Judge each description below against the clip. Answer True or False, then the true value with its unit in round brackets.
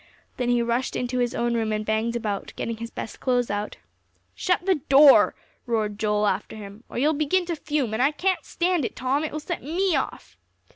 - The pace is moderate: False (210 wpm)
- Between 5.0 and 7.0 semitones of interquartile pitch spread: True (5.5 semitones)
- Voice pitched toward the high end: True (245 Hz)